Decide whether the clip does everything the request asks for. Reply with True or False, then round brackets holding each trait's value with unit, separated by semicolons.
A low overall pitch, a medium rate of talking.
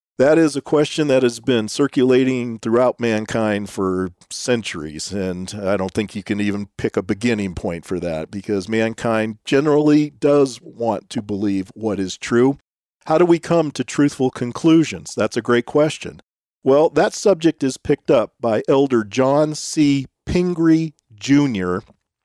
True (120 Hz; 155 wpm)